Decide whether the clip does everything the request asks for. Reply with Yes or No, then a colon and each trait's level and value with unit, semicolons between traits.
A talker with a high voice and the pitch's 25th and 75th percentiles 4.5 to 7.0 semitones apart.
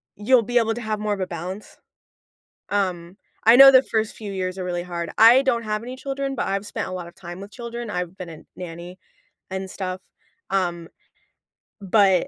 No: high, 195 Hz; average, 4.1 semitones